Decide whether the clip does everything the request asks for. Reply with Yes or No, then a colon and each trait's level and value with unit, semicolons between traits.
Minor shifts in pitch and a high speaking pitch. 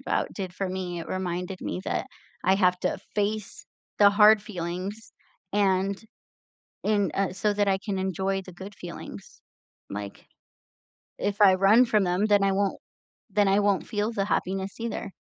Yes: narrow, 1.7 semitones; high, 195 Hz